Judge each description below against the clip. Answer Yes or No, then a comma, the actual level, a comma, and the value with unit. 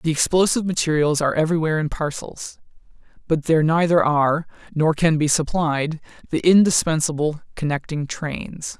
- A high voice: No, medium, 155 Hz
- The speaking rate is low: Yes, slow, 130 wpm